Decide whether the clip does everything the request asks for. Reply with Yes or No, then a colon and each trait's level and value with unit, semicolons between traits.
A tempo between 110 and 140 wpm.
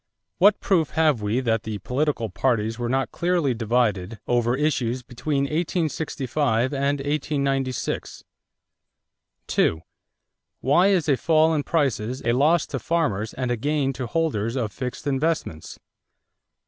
Yes: slow, 135 wpm